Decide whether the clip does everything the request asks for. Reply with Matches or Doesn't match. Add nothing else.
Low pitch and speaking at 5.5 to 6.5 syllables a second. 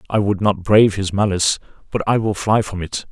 Matches